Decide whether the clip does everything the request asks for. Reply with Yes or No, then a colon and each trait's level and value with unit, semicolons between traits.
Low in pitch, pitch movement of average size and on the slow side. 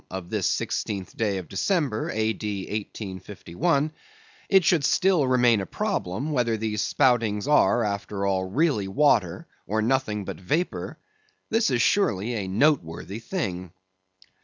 No: low, 110 Hz; wide, 6.9 semitones; slow, 130 wpm